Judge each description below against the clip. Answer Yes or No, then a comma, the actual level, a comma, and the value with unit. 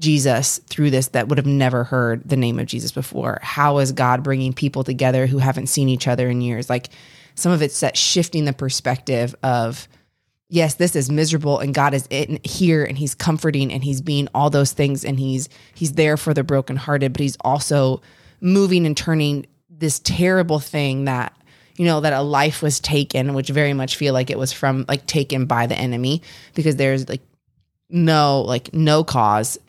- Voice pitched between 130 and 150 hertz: Yes, medium, 140 Hz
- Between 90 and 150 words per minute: No, average, 195 wpm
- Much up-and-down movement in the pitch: No, narrow, 2.5 semitones